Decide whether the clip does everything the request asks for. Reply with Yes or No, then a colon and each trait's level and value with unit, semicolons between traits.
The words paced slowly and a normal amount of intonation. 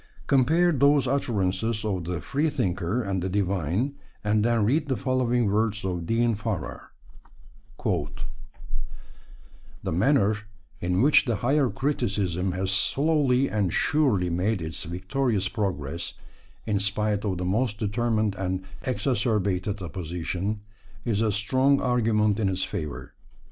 Yes: slow, 125 wpm; average, 4.9 semitones